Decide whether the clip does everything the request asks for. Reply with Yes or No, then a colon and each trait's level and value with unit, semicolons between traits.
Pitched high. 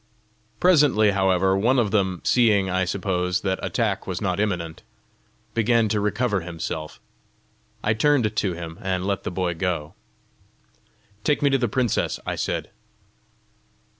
No: low, 100 Hz